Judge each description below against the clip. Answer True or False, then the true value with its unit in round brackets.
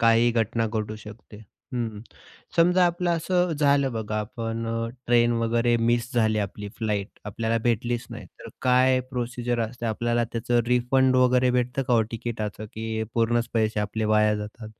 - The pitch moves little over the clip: True (2.0 semitones)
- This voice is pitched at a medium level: False (115 Hz)